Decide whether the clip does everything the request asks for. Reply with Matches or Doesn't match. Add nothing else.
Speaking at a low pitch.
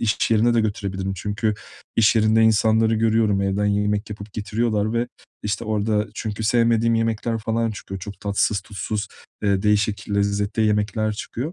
Matches